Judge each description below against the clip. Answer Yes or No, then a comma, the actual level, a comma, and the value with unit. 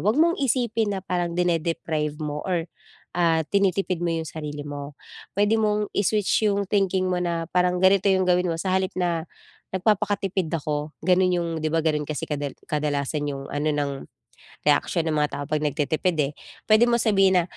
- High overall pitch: No, medium, 175 Hz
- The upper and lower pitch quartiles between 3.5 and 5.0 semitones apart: Yes, average, 4.2 semitones